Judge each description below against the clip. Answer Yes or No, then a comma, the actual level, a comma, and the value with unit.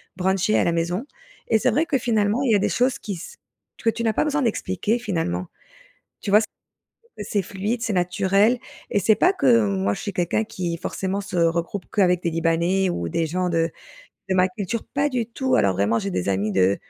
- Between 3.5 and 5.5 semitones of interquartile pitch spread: Yes, average, 5.0 semitones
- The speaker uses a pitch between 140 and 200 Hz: Yes, high, 190 Hz